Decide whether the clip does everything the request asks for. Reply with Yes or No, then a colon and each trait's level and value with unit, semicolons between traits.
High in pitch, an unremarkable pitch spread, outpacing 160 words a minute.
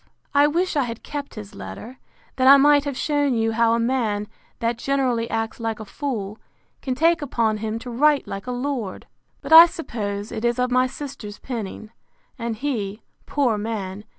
Yes: high, 235 Hz; average, 4.2 semitones; average, 185 wpm